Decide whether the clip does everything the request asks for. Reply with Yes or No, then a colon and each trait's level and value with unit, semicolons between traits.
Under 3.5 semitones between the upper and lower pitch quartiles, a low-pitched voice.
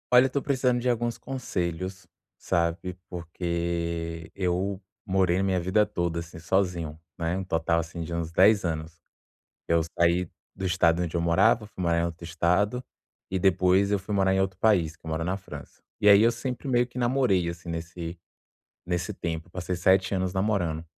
Yes: average, 2.8 semitones; very low, 90 Hz